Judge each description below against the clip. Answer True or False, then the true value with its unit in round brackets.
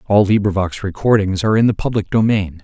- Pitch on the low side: True (100 Hz)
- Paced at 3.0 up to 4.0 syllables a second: False (6.1 syllables/s)